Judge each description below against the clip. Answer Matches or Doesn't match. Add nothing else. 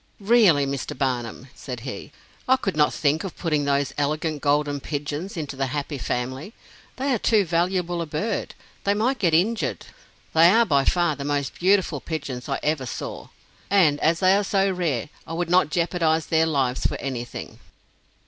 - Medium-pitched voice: Matches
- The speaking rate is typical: Matches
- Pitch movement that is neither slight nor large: Matches